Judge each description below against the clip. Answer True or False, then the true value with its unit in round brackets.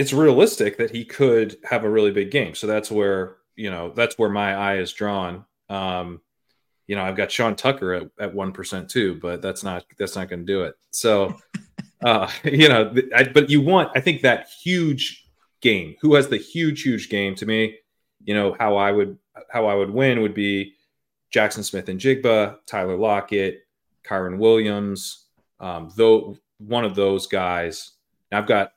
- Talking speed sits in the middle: True (185 wpm)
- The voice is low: True (105 Hz)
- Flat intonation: False (3.7 semitones)